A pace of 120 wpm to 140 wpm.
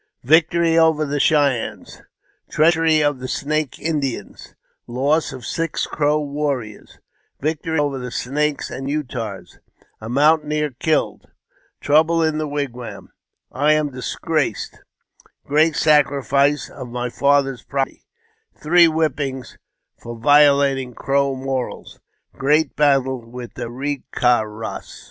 Yes: slow, 135 wpm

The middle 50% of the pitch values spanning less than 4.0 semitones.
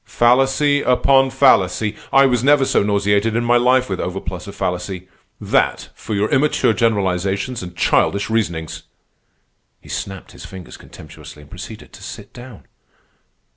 No: average, 5.2 semitones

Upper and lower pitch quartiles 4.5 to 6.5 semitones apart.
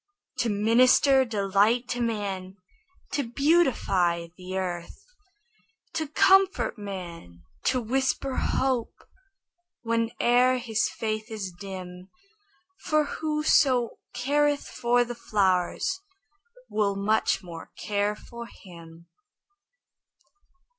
Yes: average, 5.1 semitones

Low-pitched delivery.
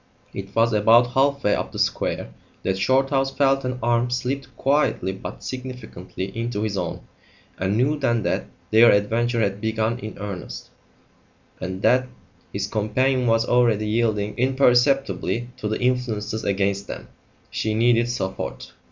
Yes: low, 115 Hz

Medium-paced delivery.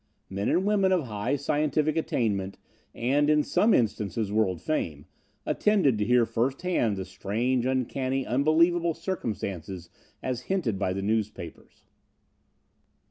No: slow, 130 wpm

